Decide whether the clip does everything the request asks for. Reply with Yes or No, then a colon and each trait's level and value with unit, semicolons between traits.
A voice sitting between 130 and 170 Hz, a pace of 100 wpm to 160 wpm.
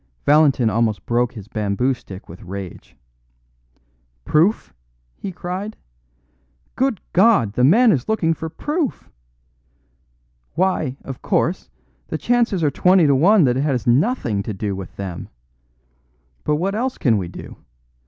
Yes: medium, 140 Hz; average, 140 wpm